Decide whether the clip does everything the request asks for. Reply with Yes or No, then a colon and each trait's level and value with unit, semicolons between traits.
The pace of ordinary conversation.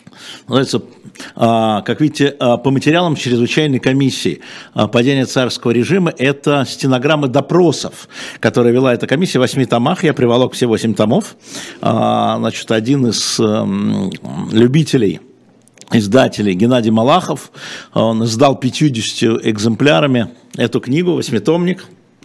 No: slow, 105 wpm